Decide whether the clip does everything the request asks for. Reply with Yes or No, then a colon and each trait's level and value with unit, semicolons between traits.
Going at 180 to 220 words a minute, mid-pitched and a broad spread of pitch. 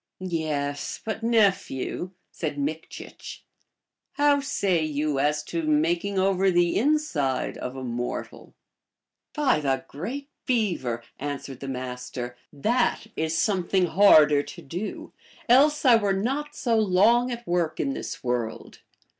No: average, 145 wpm; medium, 175 Hz; wide, 7.7 semitones